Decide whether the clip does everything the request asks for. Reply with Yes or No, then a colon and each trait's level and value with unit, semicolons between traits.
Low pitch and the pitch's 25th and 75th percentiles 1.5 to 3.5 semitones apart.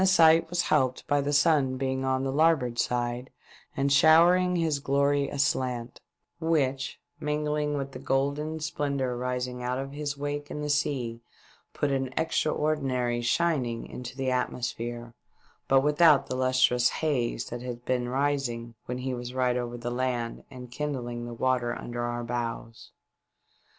Yes: low, 130 Hz; average, 3.0 semitones